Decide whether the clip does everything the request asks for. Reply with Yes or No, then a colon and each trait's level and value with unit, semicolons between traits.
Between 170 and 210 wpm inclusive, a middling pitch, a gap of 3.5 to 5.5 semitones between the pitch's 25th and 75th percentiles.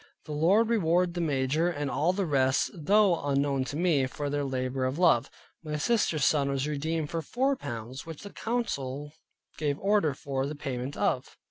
Yes: average, 180 wpm; medium, 150 Hz; average, 4.1 semitones